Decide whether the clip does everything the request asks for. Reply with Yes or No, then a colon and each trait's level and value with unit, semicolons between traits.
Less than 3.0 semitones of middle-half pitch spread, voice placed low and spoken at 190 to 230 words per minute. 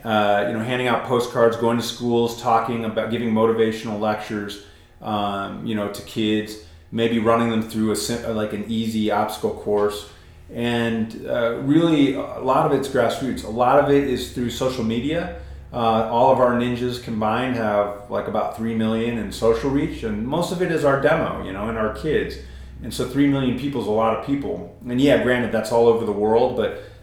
Yes: narrow, 2.5 semitones; low, 115 Hz; average, 200 wpm